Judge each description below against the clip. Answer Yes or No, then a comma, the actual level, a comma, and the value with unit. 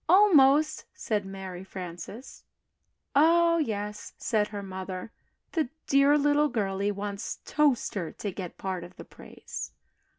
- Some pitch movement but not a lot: No, wide, 7.2 semitones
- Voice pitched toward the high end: Yes, high, 210 Hz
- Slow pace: Yes, slow, 125 wpm